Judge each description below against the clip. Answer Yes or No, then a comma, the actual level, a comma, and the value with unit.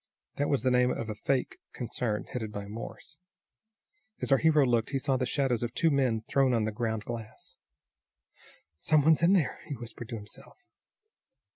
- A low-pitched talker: Yes, low, 125 Hz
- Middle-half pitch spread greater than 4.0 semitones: No, average, 3.7 semitones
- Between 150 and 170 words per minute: No, average, 180 wpm